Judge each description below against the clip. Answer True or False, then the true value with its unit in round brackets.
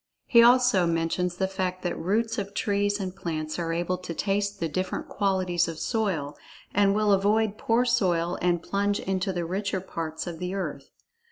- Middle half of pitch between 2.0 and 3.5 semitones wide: True (2.8 semitones)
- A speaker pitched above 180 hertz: True (190 Hz)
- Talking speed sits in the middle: True (180 wpm)